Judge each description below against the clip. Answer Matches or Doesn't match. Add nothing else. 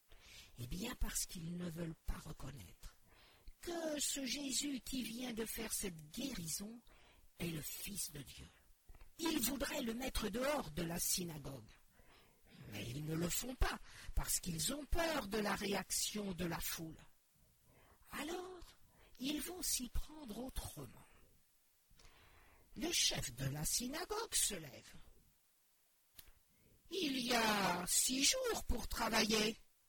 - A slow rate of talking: Matches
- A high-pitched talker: Matches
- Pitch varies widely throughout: Matches